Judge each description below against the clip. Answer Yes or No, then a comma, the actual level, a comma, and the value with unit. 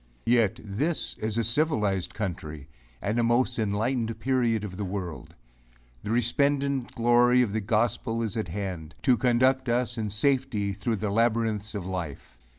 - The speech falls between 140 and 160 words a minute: Yes, average, 155 wpm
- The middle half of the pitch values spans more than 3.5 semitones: No, average, 3.2 semitones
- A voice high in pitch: No, low, 115 Hz